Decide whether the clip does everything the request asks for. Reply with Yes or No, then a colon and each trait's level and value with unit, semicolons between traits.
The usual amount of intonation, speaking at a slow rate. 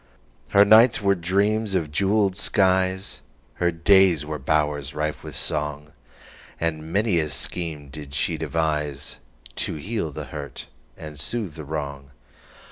Yes: average, 4.6 semitones; slow, 125 wpm